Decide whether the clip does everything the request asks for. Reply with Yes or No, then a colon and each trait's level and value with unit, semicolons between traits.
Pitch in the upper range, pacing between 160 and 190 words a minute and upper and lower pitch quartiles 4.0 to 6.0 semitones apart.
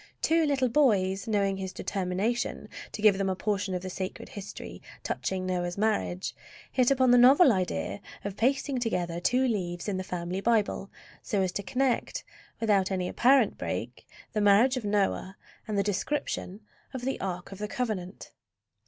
Yes: high, 200 Hz; average, 170 wpm; average, 4.4 semitones